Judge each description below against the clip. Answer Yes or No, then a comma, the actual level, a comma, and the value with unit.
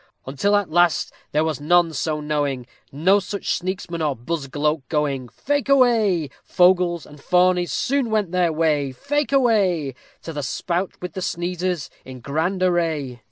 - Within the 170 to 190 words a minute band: No, average, 160 wpm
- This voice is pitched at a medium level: Yes, medium, 170 Hz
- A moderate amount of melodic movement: Yes, average, 3.8 semitones